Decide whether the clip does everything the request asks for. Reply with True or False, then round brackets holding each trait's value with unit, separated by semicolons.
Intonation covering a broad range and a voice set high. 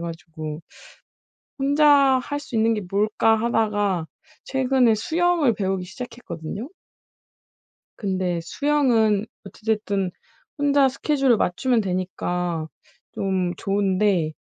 True (6.0 semitones; 210 Hz)